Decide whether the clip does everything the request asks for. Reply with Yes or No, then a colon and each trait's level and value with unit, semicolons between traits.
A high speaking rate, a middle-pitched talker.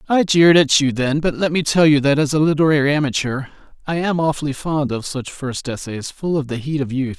Yes: fast, 240 wpm; medium, 145 Hz